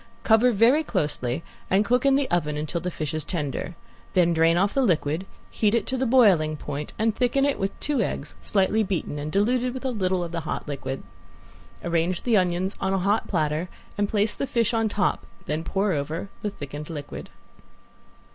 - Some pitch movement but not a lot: No, wide, 6.1 semitones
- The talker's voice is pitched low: No, high, 190 Hz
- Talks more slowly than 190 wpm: No, average, 195 wpm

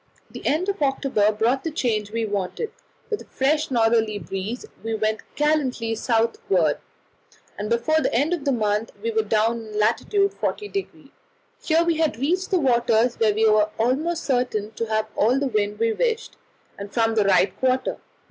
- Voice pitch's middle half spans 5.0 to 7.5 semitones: Yes, wide, 5.5 semitones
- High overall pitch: Yes, high, 230 Hz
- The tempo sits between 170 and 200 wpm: Yes, average, 175 wpm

